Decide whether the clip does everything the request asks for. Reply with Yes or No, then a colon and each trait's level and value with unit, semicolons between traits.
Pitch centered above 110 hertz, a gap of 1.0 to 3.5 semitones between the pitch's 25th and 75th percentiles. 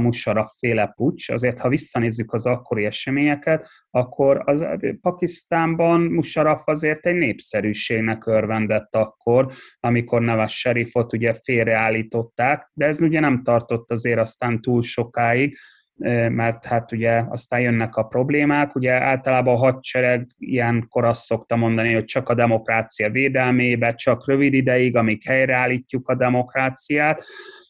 Yes: low, 125 Hz; narrow, 2.6 semitones